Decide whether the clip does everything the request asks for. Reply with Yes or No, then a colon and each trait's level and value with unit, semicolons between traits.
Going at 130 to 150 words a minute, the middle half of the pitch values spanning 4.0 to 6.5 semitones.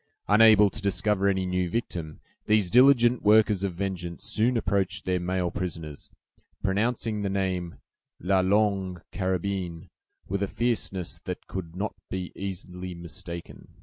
No: slow, 135 wpm; narrow, 2.6 semitones